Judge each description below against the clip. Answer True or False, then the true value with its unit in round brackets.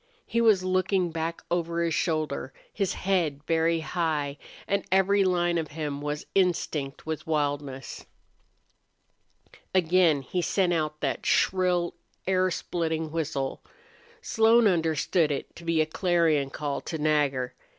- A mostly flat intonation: False (3.4 semitones)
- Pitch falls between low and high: True (165 Hz)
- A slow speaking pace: True (130 wpm)